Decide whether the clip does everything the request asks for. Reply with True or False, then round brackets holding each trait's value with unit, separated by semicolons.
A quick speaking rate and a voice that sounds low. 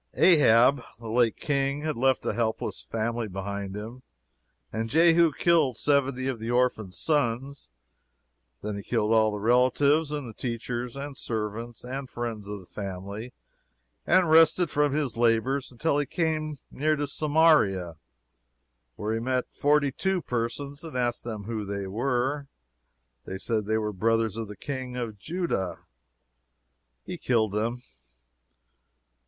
False (145 wpm; 120 Hz)